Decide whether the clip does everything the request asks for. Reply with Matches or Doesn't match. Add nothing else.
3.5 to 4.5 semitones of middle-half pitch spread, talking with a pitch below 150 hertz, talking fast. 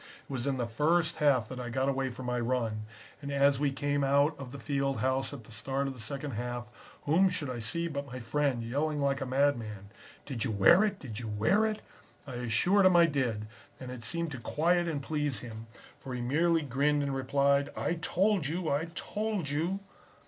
Matches